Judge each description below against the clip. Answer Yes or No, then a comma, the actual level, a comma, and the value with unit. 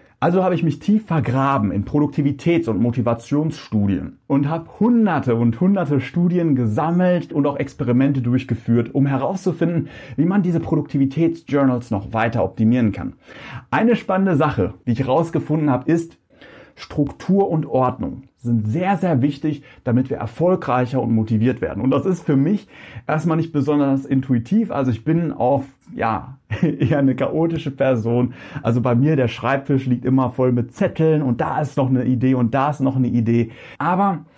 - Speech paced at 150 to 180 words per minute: Yes, average, 160 wpm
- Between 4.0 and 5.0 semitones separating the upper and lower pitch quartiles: Yes, average, 4.6 semitones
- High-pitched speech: No, medium, 140 Hz